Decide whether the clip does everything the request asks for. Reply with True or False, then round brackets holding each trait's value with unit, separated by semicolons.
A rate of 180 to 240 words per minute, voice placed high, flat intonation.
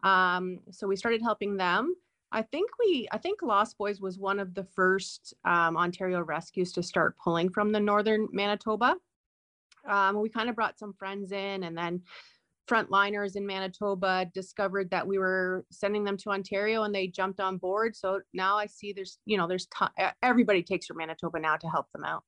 True (195 wpm; 195 Hz; 2.2 semitones)